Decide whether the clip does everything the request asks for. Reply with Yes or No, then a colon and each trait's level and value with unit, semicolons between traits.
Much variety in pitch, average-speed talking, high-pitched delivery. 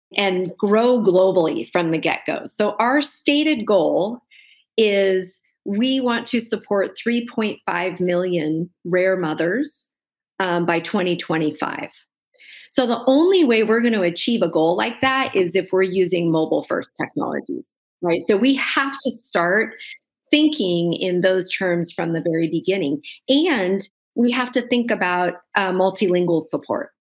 Yes: wide, 6.1 semitones; average, 145 wpm; high, 200 Hz